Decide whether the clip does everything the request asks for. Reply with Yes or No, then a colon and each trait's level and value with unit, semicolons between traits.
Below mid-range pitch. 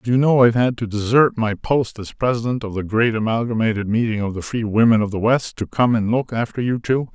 Yes: low, 115 Hz